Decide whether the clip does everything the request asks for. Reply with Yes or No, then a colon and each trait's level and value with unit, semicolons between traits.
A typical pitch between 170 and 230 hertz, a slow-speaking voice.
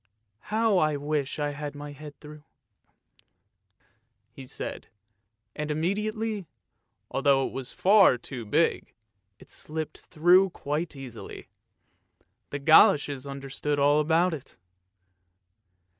No: medium, 150 Hz; slow, 115 wpm